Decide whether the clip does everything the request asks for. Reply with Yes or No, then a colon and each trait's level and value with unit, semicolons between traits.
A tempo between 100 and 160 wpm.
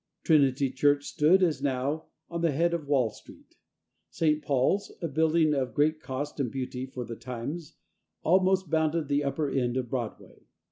No: average, 170 wpm